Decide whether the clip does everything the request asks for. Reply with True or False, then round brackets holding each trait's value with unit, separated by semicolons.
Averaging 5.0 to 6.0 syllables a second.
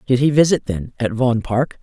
True (5.5 syllables/s)